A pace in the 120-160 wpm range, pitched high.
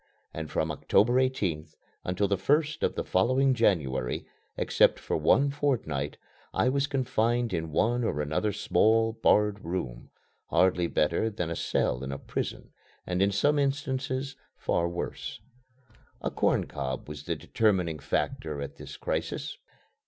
No: average, 145 wpm; low, 100 Hz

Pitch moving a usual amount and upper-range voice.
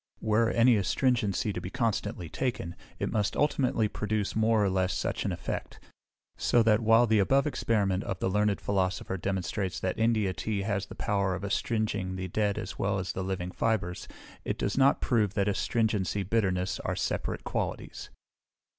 No: average, 3.0 semitones; low, 105 Hz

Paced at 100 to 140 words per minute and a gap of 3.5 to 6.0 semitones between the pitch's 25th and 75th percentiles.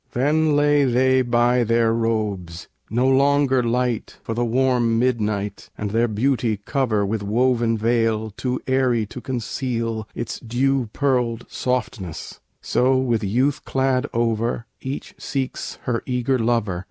No: slow, 135 wpm; narrow, 2.6 semitones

